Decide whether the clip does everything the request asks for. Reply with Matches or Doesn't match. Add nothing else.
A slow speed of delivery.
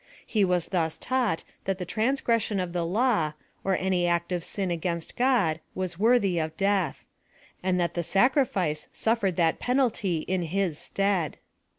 Doesn't match